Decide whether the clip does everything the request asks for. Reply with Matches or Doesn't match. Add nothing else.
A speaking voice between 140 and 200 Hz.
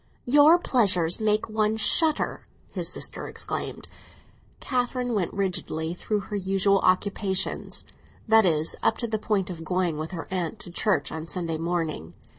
Matches